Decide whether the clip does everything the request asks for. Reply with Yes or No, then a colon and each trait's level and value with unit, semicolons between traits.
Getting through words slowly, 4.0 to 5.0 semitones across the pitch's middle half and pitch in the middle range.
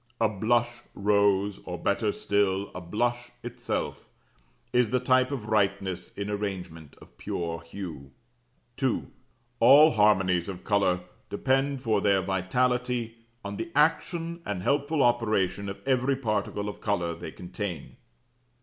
No: slow, 130 wpm; average, 4.4 semitones; low, 105 Hz